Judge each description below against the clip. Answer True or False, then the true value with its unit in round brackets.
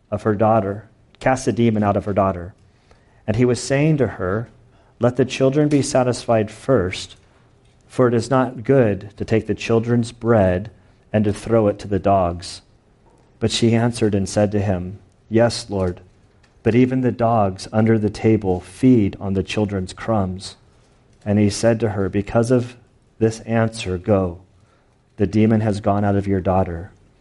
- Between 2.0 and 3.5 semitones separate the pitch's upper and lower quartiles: True (3.2 semitones)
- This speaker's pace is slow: False (170 wpm)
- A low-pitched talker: True (110 Hz)